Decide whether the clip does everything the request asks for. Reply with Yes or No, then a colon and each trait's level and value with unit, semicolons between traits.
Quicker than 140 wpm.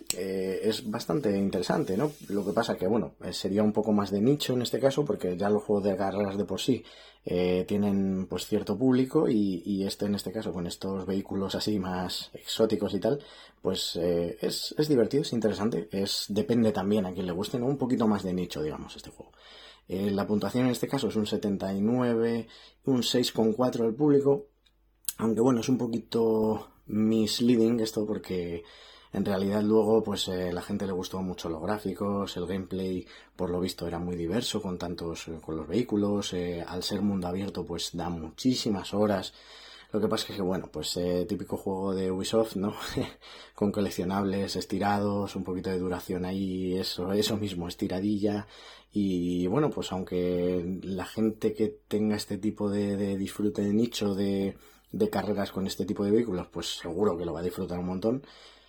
Yes: average, 185 wpm